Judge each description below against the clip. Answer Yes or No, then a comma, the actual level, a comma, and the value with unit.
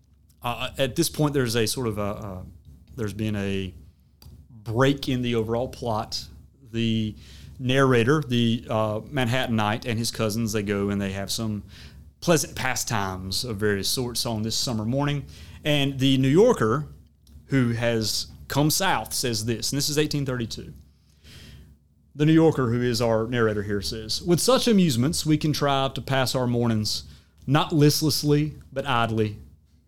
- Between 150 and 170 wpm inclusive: Yes, average, 155 wpm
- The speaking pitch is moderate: No, low, 115 Hz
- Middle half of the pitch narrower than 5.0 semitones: No, wide, 5.4 semitones